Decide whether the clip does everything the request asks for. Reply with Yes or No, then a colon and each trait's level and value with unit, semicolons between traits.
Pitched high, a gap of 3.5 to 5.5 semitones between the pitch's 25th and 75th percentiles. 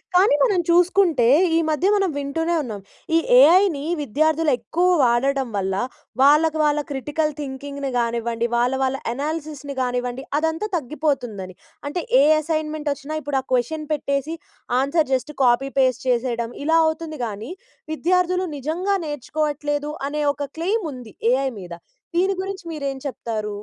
Yes: very high, 290 Hz; average, 4.0 semitones